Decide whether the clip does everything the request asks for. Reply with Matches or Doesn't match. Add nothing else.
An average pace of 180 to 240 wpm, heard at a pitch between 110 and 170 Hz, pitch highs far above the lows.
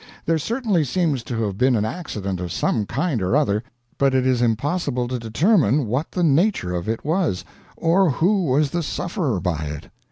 Matches